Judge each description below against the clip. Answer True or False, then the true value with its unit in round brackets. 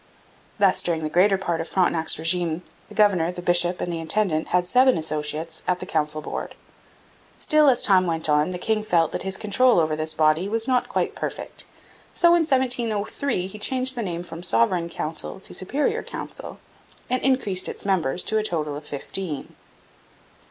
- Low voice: False (180 Hz)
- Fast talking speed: False (180 wpm)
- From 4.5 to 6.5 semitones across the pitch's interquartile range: True (4.8 semitones)